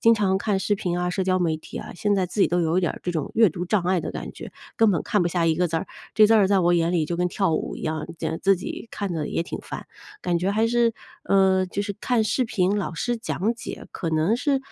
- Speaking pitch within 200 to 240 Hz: No, medium, 185 Hz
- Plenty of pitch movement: No, average, 3.3 semitones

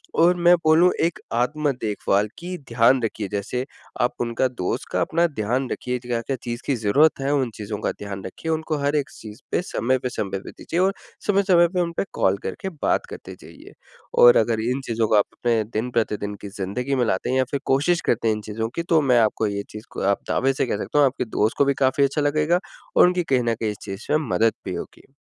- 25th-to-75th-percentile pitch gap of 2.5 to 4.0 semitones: No, wide, 5.4 semitones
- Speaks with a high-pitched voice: No, low, 125 Hz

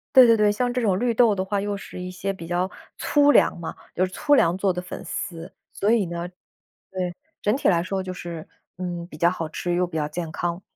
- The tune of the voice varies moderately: Yes, average, 3.1 semitones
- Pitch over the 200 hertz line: No, medium, 185 Hz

